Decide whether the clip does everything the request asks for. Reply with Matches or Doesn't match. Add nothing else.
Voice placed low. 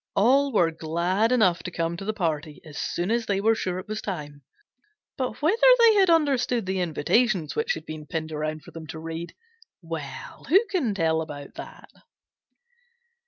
Doesn't match